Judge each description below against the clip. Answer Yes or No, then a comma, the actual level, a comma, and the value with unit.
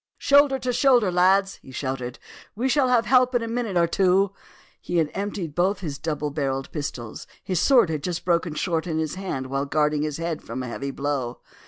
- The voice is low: No, medium, 170 Hz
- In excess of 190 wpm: Yes, fast, 205 wpm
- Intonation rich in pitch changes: Yes, wide, 5.9 semitones